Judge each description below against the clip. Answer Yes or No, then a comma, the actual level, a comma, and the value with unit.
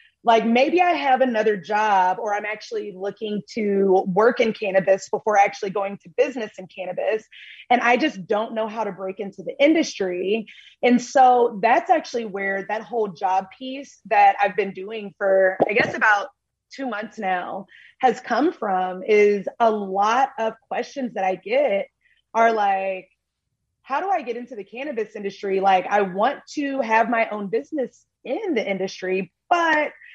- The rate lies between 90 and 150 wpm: No, average, 170 wpm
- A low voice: No, high, 215 Hz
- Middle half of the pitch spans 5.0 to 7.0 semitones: No, average, 4.0 semitones